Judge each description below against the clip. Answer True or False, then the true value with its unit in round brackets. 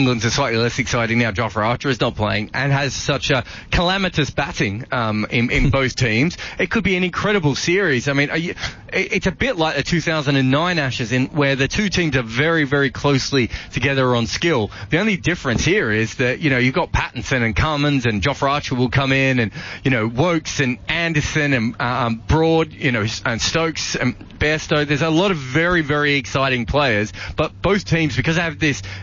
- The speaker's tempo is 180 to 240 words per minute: True (205 wpm)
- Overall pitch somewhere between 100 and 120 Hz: False (140 Hz)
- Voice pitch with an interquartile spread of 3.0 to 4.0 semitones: False (4.7 semitones)